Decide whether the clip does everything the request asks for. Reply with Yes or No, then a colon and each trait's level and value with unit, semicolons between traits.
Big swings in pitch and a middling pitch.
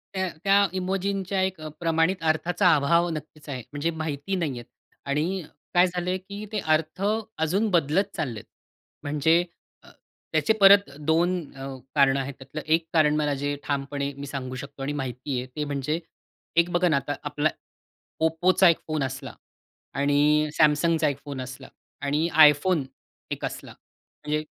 No: average, 3.6 semitones; medium, 155 Hz